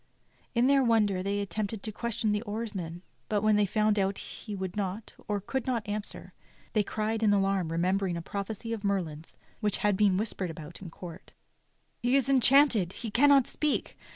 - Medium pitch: No, high, 205 Hz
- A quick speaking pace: Yes, fast, 210 wpm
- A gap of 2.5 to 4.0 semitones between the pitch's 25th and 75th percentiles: Yes, average, 2.9 semitones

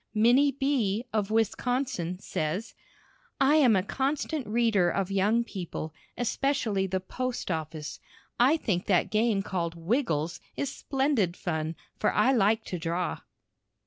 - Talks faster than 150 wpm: No, slow, 135 wpm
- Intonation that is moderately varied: No, wide, 6.0 semitones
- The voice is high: Yes, high, 210 Hz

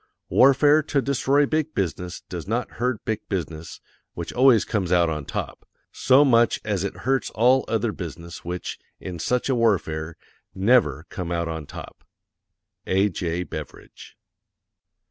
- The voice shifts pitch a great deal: Yes, wide, 6.8 semitones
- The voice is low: Yes, low, 100 Hz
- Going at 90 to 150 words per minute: Yes, average, 145 wpm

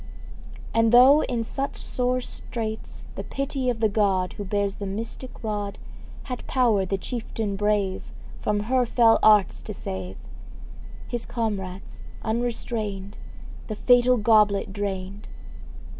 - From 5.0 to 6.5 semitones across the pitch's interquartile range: No, average, 3.2 semitones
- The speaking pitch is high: Yes, high, 215 Hz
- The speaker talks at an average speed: No, slow, 130 wpm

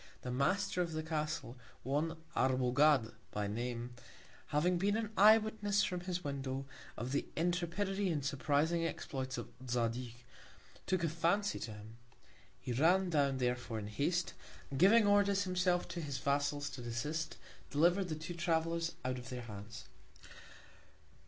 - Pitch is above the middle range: No, medium, 155 Hz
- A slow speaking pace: No, average, 150 wpm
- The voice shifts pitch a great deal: Yes, wide, 5.7 semitones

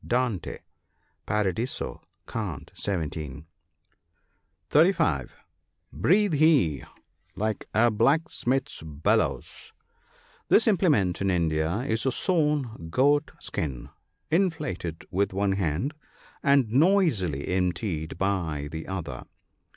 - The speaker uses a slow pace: Yes, slow, 95 wpm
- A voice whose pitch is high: No, low, 100 Hz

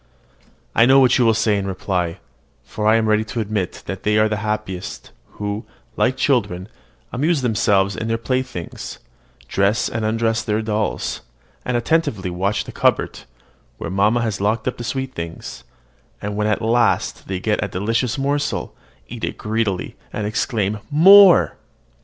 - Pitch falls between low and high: No, low, 110 Hz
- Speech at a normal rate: Yes, average, 160 wpm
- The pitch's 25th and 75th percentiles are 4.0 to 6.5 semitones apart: No, average, 2.9 semitones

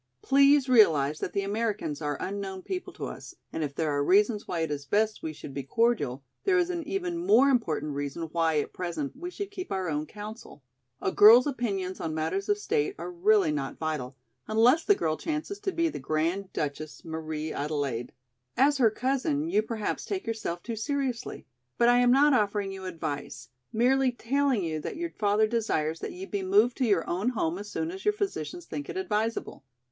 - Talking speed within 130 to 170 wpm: No, average, 200 wpm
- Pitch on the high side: Yes, high, 215 Hz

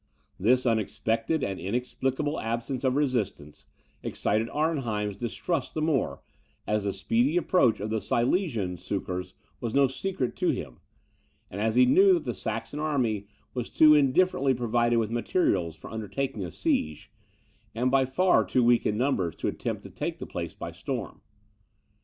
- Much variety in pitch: No, average, 4.4 semitones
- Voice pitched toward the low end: Yes, low, 120 Hz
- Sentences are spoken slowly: No, average, 160 wpm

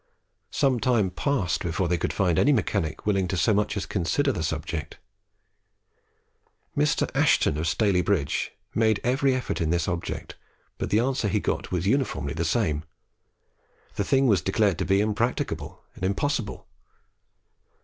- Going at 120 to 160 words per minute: Yes, average, 155 wpm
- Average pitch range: No, wide, 5.8 semitones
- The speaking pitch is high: No, low, 100 Hz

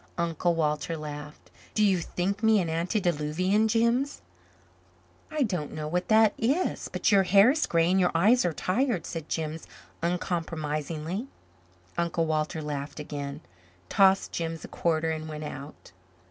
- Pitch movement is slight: No, average, 4.4 semitones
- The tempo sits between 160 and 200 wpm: No, average, 145 wpm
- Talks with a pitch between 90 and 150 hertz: No, medium, 170 Hz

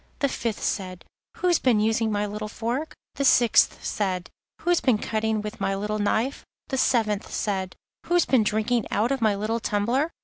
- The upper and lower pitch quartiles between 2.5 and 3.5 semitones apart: Yes, average, 3.1 semitones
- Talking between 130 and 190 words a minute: Yes, average, 175 wpm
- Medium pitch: No, high, 220 Hz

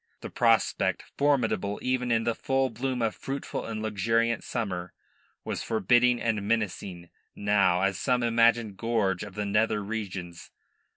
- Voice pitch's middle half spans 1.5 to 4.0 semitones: Yes, average, 3.0 semitones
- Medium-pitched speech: No, low, 110 Hz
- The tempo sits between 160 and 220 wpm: No, average, 140 wpm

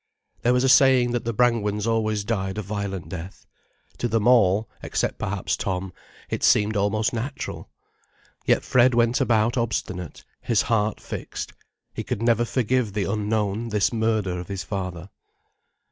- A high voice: No, low, 110 Hz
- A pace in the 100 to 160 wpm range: Yes, average, 155 wpm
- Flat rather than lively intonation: No, average, 3.0 semitones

